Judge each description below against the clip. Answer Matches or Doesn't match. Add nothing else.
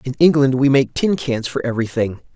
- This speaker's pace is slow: Doesn't match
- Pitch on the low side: Matches